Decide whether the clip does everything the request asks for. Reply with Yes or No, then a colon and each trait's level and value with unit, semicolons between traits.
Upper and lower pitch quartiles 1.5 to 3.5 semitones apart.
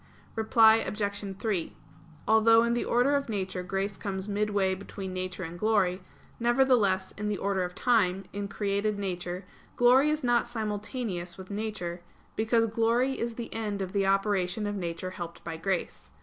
Yes: average, 3.2 semitones